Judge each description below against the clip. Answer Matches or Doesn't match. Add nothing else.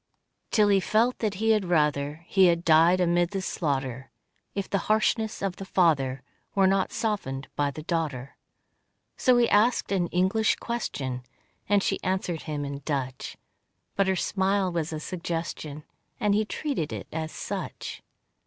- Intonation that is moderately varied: Matches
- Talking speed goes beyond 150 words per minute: Matches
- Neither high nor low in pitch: Matches